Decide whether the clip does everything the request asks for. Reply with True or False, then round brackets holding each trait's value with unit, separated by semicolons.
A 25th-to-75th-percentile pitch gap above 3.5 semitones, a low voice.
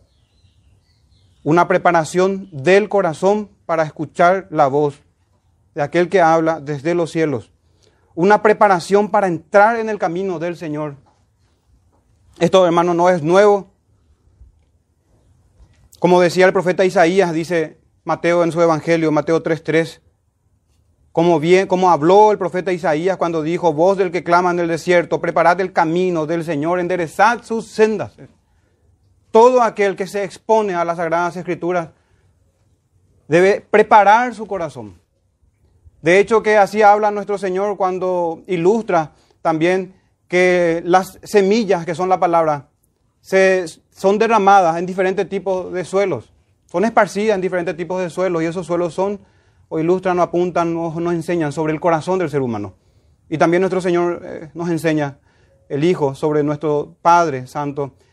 False (5.2 semitones; 170 Hz)